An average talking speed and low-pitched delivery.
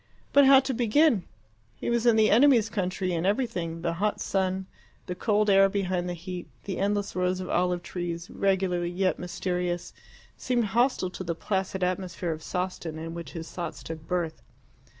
No: average, 175 wpm; medium, 185 Hz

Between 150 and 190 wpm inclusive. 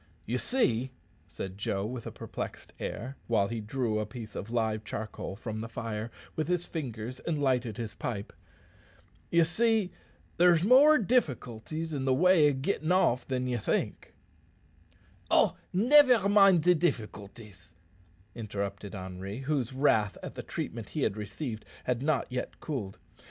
Yes: average, 155 wpm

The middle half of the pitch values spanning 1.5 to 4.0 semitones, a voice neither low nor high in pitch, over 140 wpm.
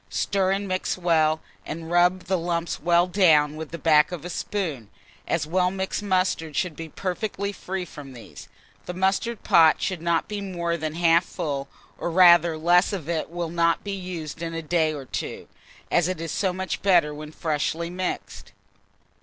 Yes: narrow, 2.6 semitones; medium, 170 Hz; average, 185 wpm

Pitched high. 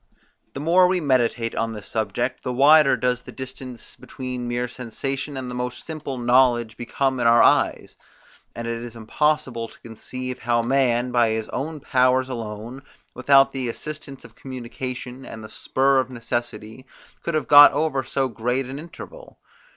No: low, 125 Hz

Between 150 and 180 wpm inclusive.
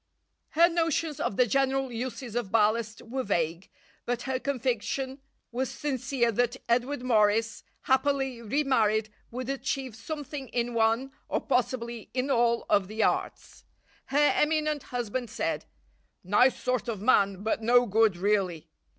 No: average, 140 wpm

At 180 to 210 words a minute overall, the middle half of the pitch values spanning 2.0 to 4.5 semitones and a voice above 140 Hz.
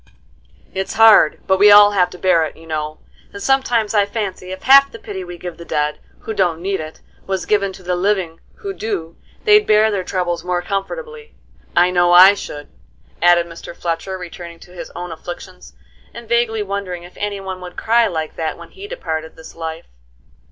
Yes: average, 195 wpm; average, 3.4 semitones; medium, 185 Hz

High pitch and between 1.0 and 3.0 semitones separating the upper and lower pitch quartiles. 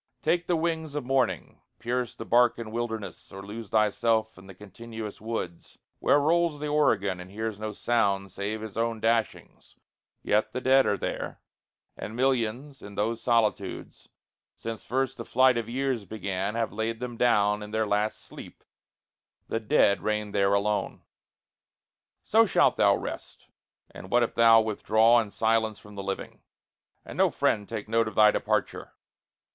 No: low, 110 Hz; average, 2.7 semitones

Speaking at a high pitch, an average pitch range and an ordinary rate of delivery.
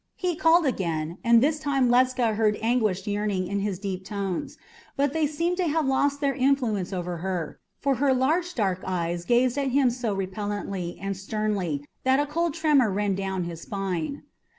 No: high, 215 Hz; wide, 6.5 semitones; average, 180 wpm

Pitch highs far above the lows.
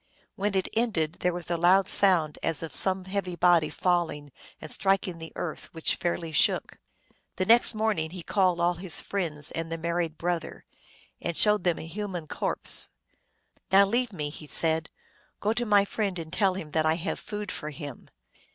No: average, 3.3 semitones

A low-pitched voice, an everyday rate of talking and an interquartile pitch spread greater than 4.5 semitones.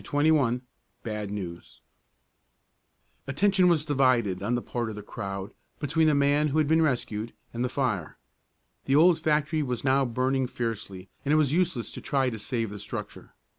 Yes: low, 130 Hz; average, 175 wpm; average, 5.1 semitones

